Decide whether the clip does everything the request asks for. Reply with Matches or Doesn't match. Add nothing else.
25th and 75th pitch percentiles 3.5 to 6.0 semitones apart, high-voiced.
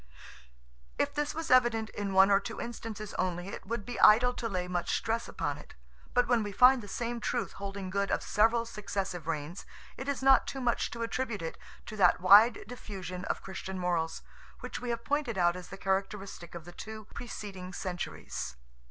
Matches